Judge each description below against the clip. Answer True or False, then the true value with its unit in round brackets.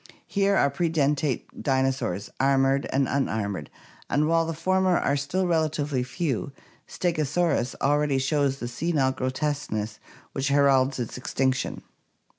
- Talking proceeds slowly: True (120 wpm)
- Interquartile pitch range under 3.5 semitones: True (3.0 semitones)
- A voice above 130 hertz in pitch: True (140 Hz)